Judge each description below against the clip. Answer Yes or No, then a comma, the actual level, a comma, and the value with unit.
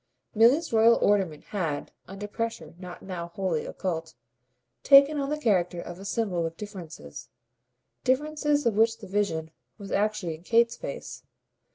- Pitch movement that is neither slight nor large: Yes, average, 5.0 semitones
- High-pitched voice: Yes, high, 205 Hz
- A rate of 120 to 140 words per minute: No, average, 150 wpm